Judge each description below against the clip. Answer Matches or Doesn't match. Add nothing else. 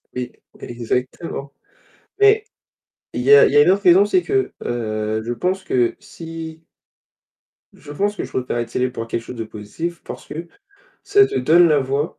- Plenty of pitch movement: Matches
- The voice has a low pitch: Doesn't match